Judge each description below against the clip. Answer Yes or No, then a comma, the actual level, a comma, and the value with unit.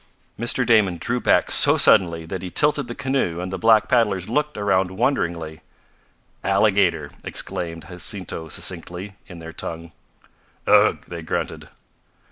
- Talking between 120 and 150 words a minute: Yes, slow, 135 wpm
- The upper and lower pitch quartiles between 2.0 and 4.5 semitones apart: No, average, 5.0 semitones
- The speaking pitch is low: Yes, very low, 95 Hz